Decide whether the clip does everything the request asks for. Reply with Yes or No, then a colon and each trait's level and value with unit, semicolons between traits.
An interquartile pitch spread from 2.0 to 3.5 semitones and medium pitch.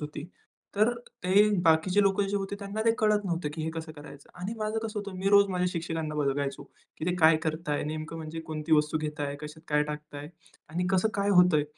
No: average, 4.6 semitones; medium, 165 Hz